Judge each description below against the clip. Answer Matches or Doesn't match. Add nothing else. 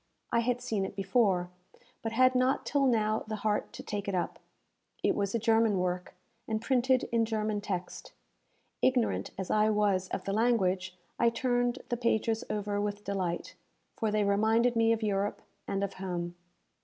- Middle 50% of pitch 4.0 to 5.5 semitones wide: Doesn't match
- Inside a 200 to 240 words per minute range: Doesn't match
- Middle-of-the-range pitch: Doesn't match